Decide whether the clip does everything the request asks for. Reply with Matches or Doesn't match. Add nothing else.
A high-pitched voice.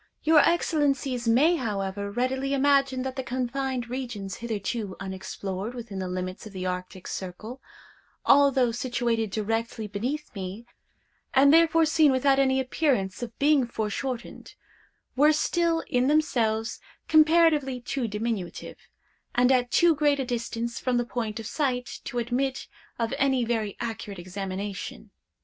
Matches